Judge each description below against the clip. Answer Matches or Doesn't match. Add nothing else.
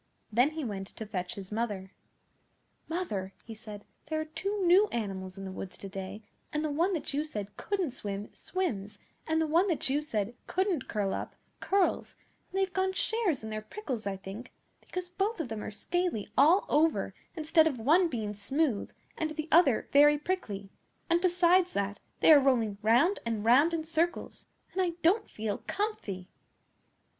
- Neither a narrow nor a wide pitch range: Doesn't match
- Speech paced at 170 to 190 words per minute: Matches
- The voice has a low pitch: Doesn't match